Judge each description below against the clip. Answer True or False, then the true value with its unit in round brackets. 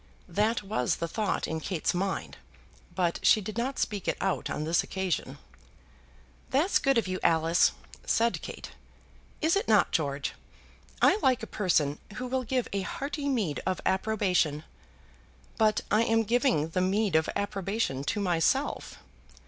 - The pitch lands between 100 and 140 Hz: False (200 Hz)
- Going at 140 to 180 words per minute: True (155 wpm)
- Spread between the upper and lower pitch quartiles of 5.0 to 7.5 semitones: True (5.4 semitones)